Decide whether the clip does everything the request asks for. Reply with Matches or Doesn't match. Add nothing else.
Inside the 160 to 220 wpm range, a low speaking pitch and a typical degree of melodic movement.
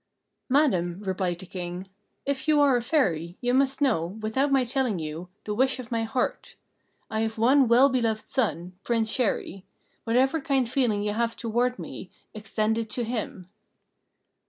Doesn't match